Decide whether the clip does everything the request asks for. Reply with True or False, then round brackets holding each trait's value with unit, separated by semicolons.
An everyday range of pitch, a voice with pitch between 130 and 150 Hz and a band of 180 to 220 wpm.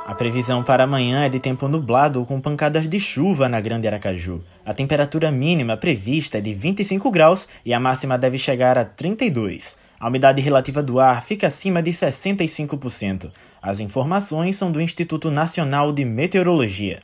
False (5.0 semitones; 135 Hz; 165 wpm)